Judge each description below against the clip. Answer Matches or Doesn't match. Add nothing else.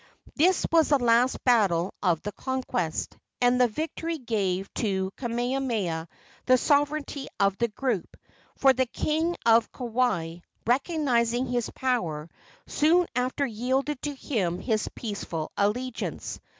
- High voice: Matches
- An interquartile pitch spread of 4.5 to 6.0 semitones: Matches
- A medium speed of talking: Doesn't match